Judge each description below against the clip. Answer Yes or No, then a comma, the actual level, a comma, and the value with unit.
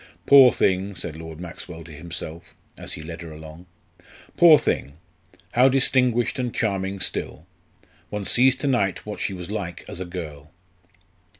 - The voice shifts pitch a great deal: Yes, wide, 6.5 semitones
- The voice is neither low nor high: No, very low, 95 Hz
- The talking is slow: No, average, 160 wpm